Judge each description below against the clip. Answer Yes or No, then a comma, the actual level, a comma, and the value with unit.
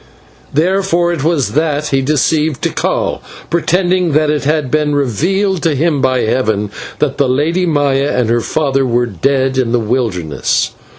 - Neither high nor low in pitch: Yes, medium, 145 Hz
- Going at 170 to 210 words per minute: No, average, 160 wpm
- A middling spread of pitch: Yes, average, 3.9 semitones